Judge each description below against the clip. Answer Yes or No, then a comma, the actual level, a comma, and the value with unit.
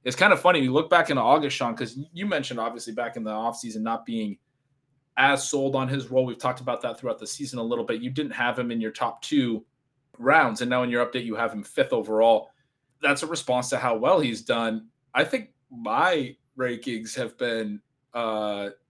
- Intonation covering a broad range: No, average, 3.2 semitones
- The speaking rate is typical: No, fast, 220 wpm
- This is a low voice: Yes, low, 125 Hz